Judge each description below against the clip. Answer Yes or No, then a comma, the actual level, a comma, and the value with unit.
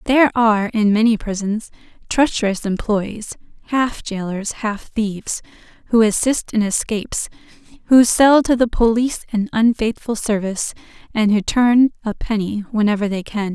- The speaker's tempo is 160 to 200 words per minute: No, slow, 135 wpm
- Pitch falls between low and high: No, high, 220 Hz